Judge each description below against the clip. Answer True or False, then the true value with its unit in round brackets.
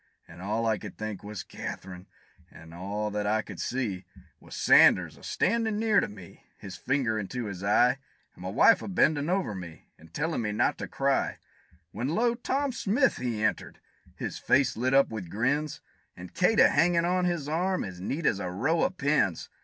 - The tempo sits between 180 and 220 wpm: True (195 wpm)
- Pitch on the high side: False (120 Hz)